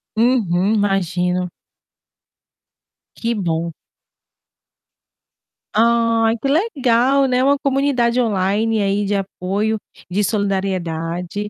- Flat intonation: No, average, 4.0 semitones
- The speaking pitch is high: Yes, high, 210 Hz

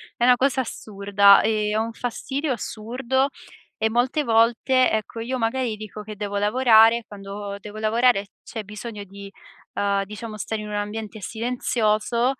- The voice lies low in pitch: No, high, 220 Hz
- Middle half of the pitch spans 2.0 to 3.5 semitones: Yes, narrow, 2.6 semitones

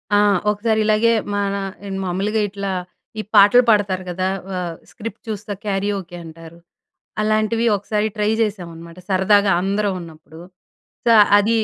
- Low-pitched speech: No, high, 200 Hz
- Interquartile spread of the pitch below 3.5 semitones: Yes, narrow, 2.4 semitones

